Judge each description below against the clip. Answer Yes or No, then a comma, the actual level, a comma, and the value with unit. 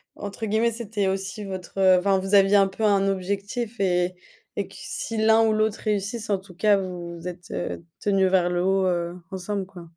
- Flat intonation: Yes, narrow, 2.2 semitones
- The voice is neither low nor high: No, high, 195 Hz